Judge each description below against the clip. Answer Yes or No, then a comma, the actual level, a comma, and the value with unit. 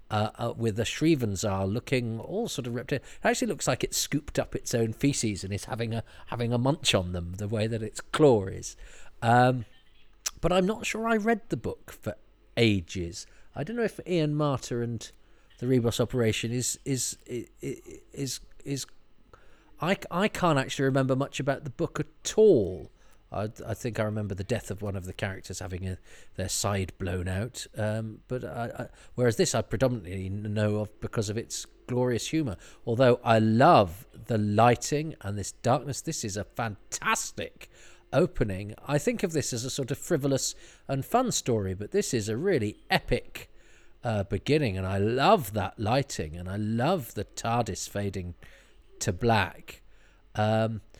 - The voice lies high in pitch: No, low, 115 Hz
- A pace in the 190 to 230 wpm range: No, average, 180 wpm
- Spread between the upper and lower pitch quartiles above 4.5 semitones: Yes, average, 4.9 semitones